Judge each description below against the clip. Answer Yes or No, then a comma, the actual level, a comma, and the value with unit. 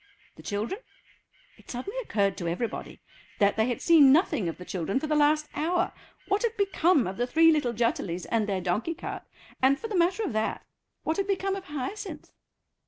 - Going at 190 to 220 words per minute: Yes, average, 195 wpm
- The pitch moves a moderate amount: No, wide, 8.9 semitones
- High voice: Yes, very high, 290 Hz